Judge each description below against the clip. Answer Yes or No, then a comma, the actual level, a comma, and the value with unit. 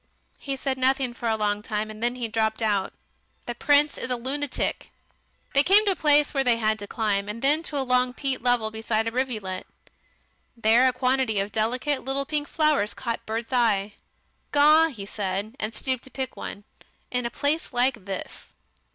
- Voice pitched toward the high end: Yes, high, 245 Hz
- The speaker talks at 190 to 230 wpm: Yes, average, 195 wpm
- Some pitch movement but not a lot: Yes, average, 3.8 semitones